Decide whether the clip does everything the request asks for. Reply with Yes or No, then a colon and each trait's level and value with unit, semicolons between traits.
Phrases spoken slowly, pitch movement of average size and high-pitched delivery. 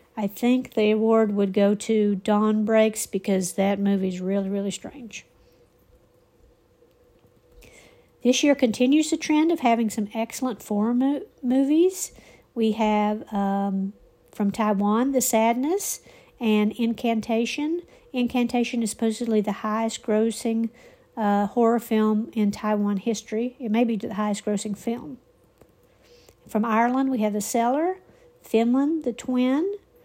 Yes: slow, 130 wpm; average, 3.1 semitones; high, 225 Hz